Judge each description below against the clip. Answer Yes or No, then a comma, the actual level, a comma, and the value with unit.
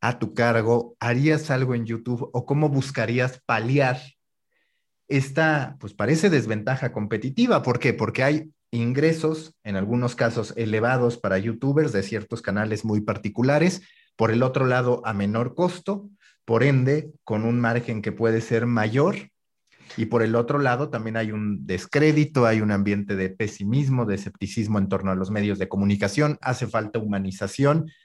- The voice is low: Yes, low, 120 Hz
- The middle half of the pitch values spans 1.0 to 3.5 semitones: No, average, 4.5 semitones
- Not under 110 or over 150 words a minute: No, average, 160 wpm